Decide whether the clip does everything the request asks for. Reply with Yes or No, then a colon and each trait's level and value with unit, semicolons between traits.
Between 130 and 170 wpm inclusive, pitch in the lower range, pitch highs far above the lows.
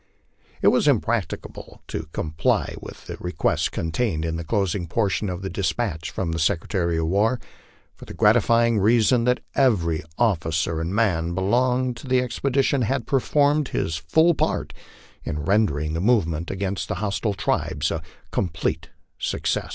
Yes: average, 155 wpm; low, 100 Hz; wide, 6.5 semitones